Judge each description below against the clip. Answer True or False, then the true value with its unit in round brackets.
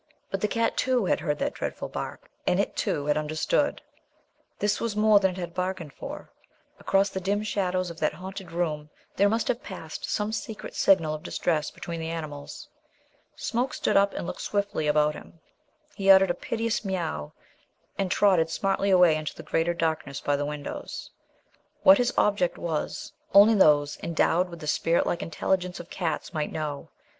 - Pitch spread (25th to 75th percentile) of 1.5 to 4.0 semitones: False (4.4 semitones)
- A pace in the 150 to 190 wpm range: True (180 wpm)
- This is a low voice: False (180 Hz)